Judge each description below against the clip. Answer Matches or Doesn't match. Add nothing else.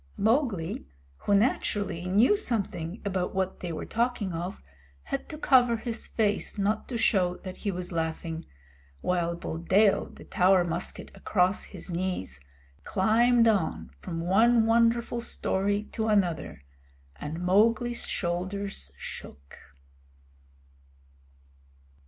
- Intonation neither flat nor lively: Matches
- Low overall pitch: Doesn't match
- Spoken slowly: Matches